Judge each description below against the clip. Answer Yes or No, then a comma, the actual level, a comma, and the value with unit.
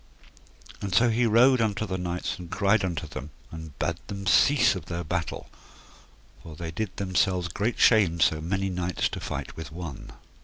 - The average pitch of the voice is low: Yes, very low, 90 Hz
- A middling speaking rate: Yes, average, 180 wpm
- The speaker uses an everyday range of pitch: Yes, average, 3.6 semitones